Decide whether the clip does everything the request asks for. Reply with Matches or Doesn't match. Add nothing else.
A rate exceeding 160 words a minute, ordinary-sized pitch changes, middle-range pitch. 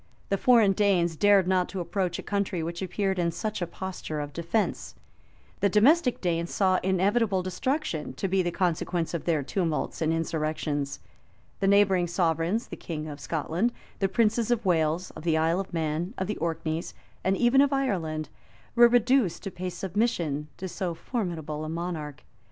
Matches